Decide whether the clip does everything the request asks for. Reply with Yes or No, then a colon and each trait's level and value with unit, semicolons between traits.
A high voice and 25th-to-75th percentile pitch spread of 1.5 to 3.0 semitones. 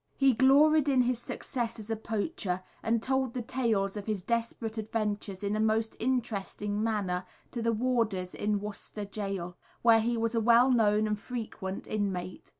Yes: high, 220 Hz; average, 2.7 semitones